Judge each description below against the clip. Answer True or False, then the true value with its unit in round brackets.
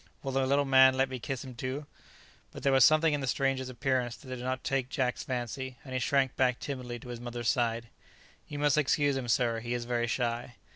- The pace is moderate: False (230 wpm)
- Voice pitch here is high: False (130 Hz)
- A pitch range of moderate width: False (1.9 semitones)